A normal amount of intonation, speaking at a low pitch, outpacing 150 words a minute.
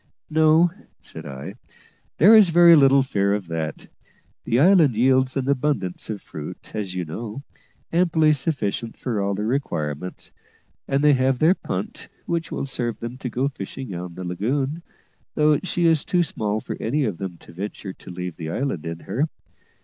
No: wide, 7.5 semitones; low, 125 Hz; average, 175 wpm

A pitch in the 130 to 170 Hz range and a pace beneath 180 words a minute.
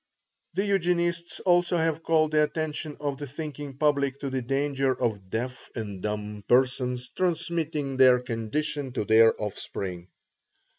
Yes: medium, 140 Hz; average, 140 wpm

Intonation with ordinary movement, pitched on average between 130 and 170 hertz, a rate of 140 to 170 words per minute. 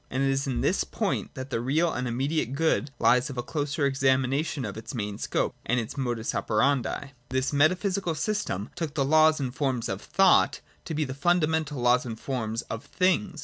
No: average, 4.2 semitones; low, 135 Hz; average, 200 wpm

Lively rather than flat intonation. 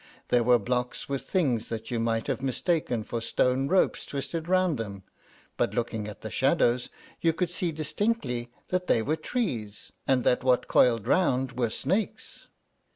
Yes: wide, 5.9 semitones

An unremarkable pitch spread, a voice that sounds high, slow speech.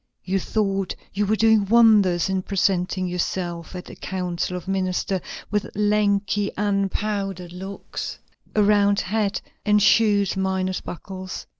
No: narrow, 1.9 semitones; high, 195 Hz; slow, 130 wpm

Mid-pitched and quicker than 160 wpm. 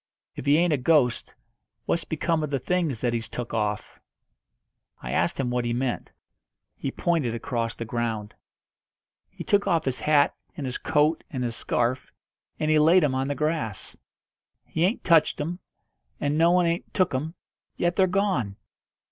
Yes: medium, 145 Hz; average, 175 wpm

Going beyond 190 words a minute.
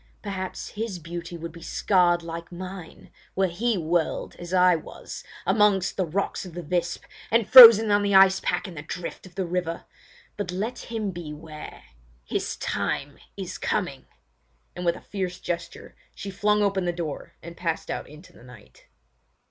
No: average, 170 wpm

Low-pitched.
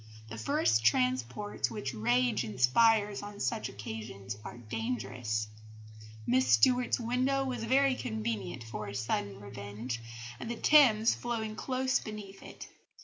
Yes: low, 125 Hz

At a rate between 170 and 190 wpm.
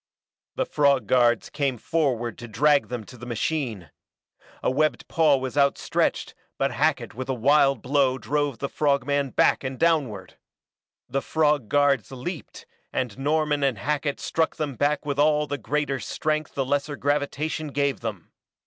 No: average, 160 wpm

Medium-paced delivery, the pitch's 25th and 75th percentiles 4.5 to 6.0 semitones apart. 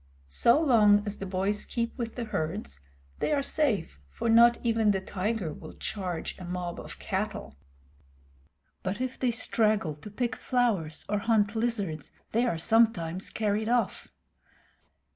No: average, 150 wpm; average, 4.0 semitones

